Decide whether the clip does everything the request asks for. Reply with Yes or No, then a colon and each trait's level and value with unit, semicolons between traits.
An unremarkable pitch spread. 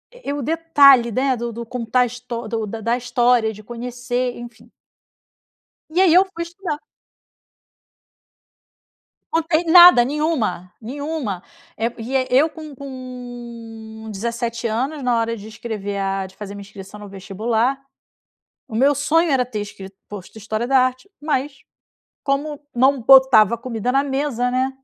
Yes: average, 3.8 semitones